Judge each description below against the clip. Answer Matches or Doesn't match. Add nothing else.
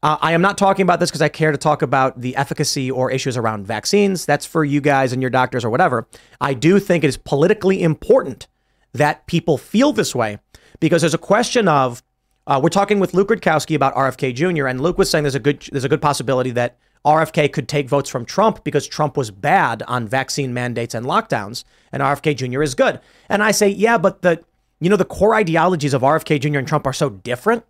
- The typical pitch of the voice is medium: Matches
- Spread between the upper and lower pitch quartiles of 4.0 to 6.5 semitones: Matches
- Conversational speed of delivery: Doesn't match